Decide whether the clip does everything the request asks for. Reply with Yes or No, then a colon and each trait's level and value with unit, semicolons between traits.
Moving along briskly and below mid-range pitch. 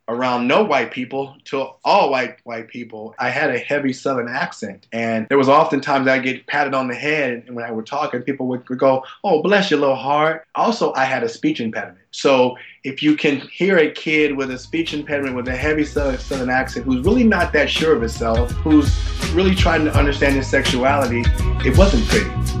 Yes: fast, 210 wpm; low, 130 Hz